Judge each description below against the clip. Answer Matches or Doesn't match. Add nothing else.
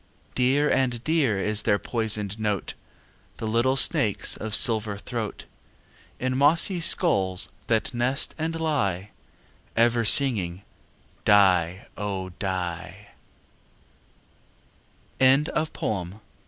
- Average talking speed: Doesn't match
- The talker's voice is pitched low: Matches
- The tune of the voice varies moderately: Matches